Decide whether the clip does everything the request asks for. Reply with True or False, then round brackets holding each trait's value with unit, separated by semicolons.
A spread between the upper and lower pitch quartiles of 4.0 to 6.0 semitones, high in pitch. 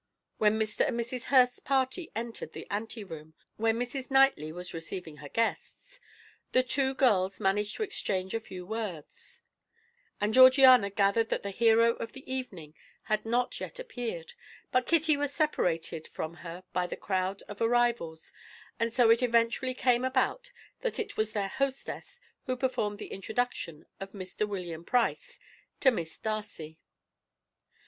True (5.2 semitones; 225 Hz)